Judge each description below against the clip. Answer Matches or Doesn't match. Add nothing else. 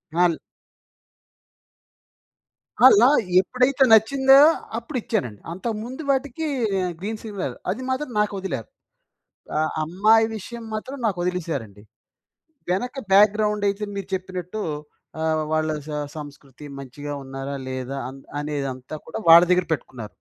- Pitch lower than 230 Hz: Matches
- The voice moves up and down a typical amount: Doesn't match